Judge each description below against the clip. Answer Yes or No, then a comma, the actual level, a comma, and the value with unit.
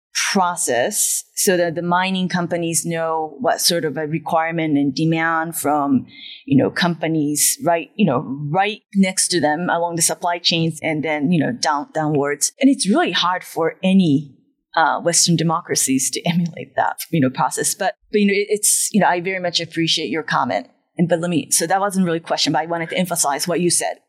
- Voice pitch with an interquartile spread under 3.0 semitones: Yes, narrow, 2.4 semitones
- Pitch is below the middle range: No, medium, 170 Hz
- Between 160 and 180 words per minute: No, fast, 205 wpm